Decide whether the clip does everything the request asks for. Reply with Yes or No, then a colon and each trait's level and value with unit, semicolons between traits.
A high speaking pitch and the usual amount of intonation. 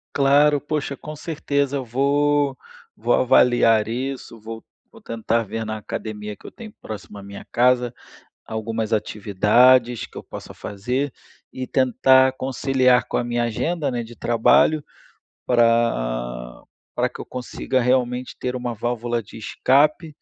No: low, 125 Hz; average, 3.2 semitones